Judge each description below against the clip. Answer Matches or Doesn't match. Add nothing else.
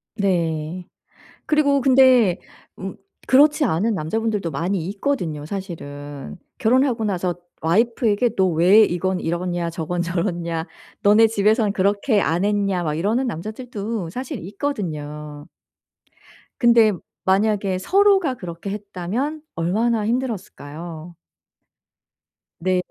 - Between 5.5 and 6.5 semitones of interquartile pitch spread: Doesn't match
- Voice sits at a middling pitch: Doesn't match